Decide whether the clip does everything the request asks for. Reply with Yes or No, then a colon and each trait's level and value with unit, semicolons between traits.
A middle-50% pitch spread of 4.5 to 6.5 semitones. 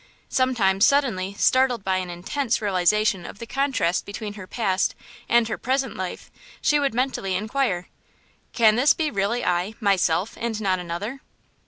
Yes: average, 5.2 semitones